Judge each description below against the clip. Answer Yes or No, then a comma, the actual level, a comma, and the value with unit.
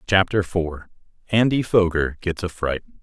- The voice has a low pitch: Yes, very low, 95 Hz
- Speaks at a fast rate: No, slow, 120 wpm